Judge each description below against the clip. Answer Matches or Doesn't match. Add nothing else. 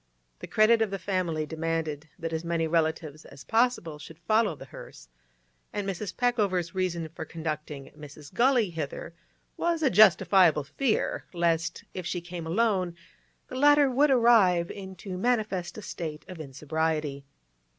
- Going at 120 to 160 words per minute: Matches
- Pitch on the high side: Doesn't match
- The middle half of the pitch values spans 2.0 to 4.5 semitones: Doesn't match